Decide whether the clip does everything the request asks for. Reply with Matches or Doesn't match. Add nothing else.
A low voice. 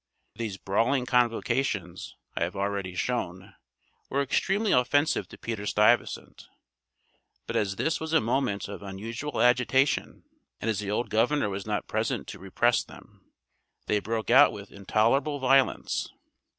Matches